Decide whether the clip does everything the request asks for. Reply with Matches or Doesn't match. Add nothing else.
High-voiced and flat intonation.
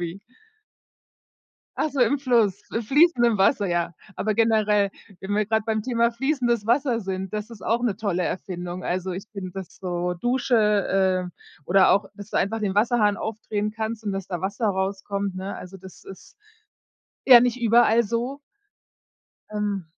Doesn't match